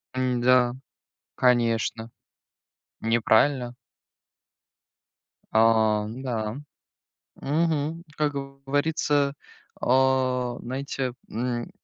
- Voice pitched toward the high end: No, low, 125 Hz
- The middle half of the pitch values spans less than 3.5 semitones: Yes, average, 2.9 semitones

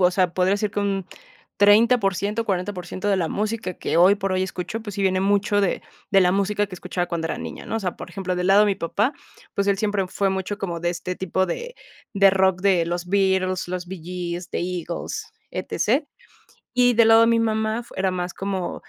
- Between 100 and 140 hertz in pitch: No, high, 190 Hz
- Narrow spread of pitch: Yes, narrow, 2.2 semitones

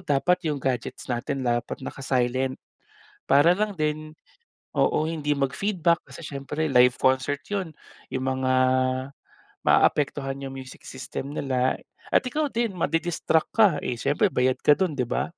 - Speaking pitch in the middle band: Yes, medium, 145 Hz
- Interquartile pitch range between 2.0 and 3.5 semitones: No, average, 4.1 semitones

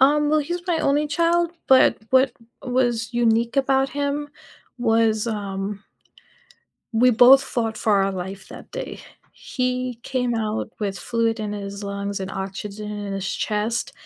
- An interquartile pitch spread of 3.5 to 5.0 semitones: Yes, average, 4.5 semitones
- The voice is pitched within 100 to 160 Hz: No, high, 230 Hz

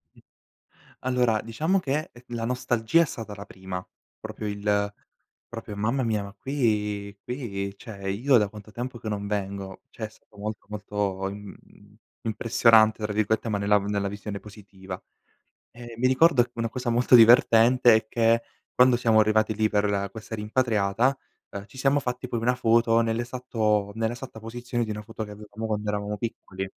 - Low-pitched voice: Yes, low, 110 Hz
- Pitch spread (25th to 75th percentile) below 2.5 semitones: No, average, 2.8 semitones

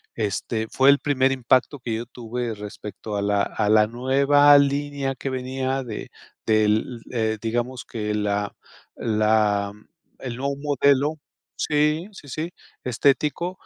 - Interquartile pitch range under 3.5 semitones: No, average, 4.4 semitones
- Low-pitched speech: Yes, low, 125 Hz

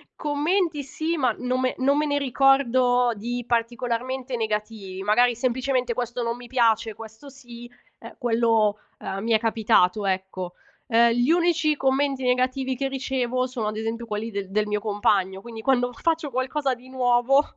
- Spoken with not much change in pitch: No, average, 3.0 semitones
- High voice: Yes, high, 245 Hz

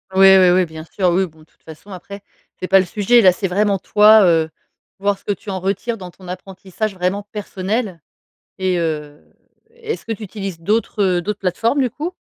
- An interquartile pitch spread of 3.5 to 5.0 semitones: No, average, 2.8 semitones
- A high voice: Yes, high, 195 Hz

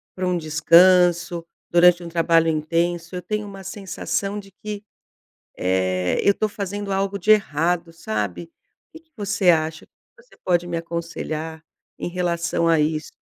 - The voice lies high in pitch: No, medium, 175 Hz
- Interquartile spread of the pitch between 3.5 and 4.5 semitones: No, average, 3.0 semitones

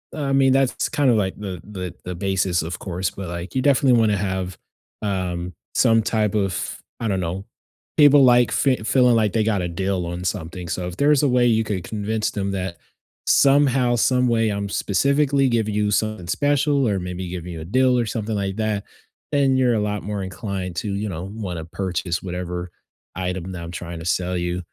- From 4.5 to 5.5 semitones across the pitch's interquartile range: Yes, average, 5.0 semitones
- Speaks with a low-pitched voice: Yes, low, 100 Hz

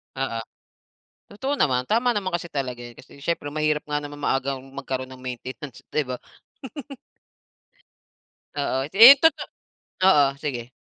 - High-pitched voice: No, medium, 145 Hz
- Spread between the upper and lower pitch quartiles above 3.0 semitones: Yes, average, 4.7 semitones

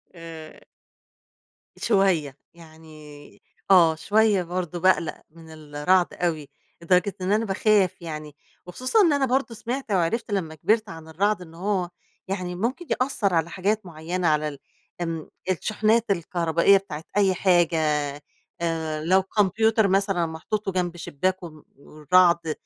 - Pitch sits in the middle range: Yes, medium, 180 Hz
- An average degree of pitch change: Yes, average, 3.9 semitones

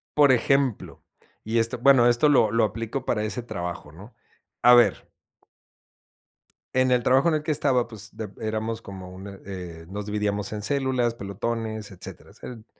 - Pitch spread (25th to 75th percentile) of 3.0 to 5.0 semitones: Yes, average, 3.5 semitones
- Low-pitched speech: Yes, low, 115 Hz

